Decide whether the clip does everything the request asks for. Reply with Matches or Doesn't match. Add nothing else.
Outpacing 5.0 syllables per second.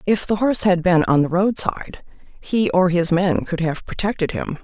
Doesn't match